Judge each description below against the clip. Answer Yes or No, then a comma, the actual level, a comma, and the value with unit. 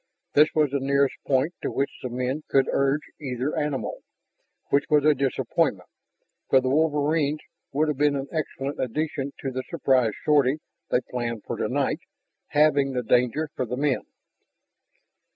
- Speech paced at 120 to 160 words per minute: Yes, average, 155 wpm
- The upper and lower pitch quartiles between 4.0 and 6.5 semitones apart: No, narrow, 2.6 semitones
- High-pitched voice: No, medium, 140 Hz